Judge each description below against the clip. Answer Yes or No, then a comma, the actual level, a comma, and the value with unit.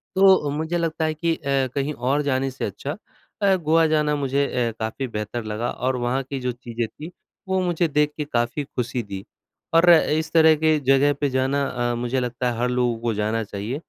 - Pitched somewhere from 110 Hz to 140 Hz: Yes, low, 135 Hz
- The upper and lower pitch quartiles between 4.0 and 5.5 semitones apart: Yes, average, 4.3 semitones